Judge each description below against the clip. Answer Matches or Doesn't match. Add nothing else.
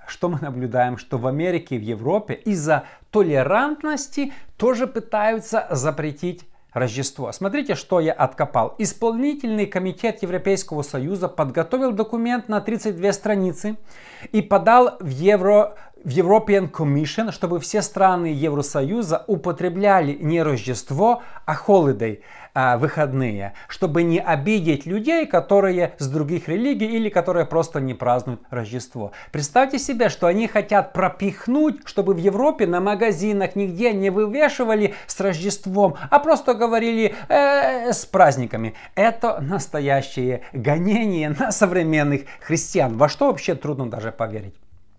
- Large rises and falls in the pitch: Matches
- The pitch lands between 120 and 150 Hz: Doesn't match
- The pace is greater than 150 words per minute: Doesn't match